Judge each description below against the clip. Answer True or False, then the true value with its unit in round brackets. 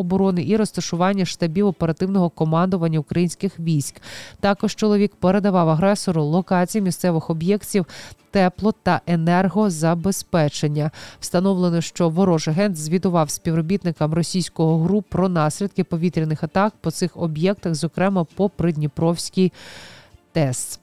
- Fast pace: False (105 wpm)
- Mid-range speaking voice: True (175 Hz)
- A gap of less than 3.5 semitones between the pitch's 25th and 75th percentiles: True (2.9 semitones)